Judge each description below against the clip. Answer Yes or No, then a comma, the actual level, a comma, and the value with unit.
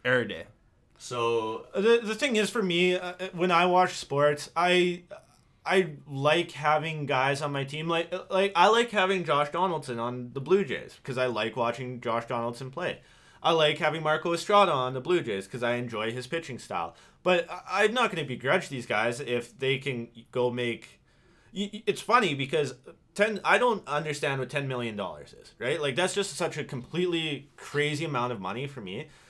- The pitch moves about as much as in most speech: No, wide, 6.3 semitones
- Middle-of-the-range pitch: Yes, medium, 150 Hz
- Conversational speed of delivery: Yes, average, 190 wpm